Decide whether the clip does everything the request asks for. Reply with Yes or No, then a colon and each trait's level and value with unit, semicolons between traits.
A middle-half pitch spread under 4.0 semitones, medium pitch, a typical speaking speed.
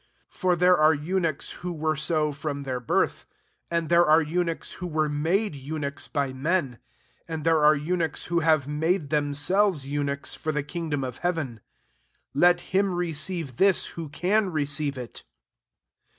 Yes: average, 3.3 semitones; medium, 155 Hz; average, 170 wpm